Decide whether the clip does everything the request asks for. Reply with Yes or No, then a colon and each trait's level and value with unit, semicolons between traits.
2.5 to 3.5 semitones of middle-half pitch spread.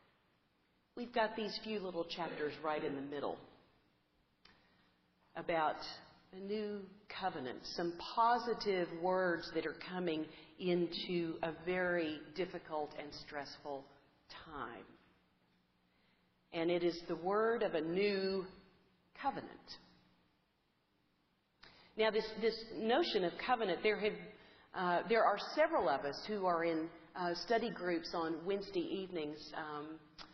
No: average, 5.2 semitones